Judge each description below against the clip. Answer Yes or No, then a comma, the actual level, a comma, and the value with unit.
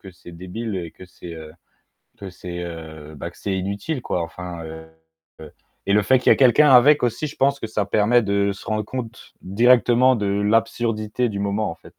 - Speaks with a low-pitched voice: Yes, low, 100 Hz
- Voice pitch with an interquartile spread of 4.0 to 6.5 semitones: Yes, average, 5.2 semitones